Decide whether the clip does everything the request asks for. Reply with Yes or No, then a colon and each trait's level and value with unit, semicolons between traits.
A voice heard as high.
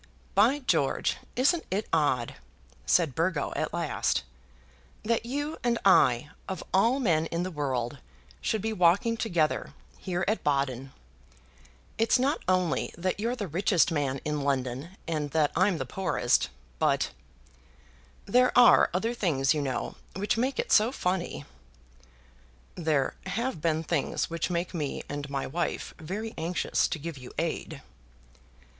No: medium, 175 Hz